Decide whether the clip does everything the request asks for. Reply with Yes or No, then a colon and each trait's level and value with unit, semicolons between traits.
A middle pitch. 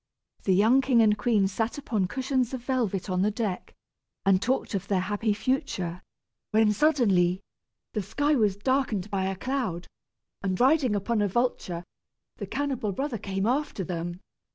No: high, 210 Hz